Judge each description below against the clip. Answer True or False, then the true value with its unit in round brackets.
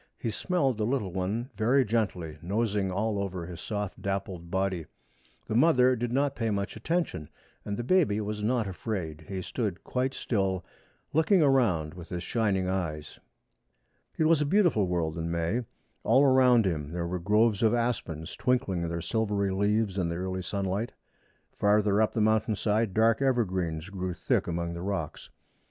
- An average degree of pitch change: True (4.6 semitones)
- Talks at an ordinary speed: True (170 wpm)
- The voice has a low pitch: True (100 Hz)